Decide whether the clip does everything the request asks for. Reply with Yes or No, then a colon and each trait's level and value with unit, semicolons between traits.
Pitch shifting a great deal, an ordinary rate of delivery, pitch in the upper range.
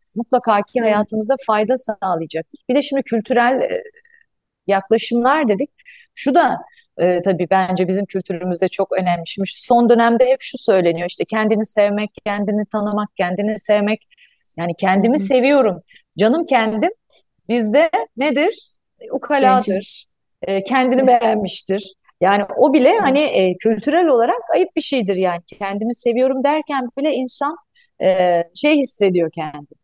Yes: wide, 6.3 semitones; average, 120 wpm; high, 230 Hz